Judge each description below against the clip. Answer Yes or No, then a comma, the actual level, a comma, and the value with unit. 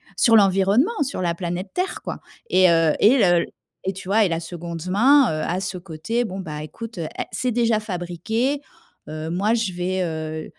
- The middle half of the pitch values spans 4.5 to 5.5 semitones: Yes, average, 4.8 semitones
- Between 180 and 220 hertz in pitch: Yes, medium, 185 Hz